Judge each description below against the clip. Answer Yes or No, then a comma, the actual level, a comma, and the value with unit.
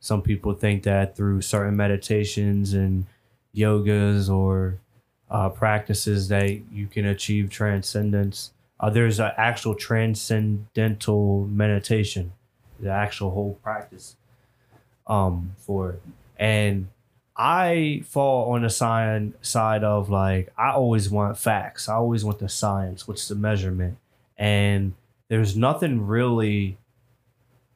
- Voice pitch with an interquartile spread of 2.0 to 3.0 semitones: Yes, narrow, 2.4 semitones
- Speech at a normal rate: No, slow, 120 wpm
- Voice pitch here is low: Yes, low, 105 Hz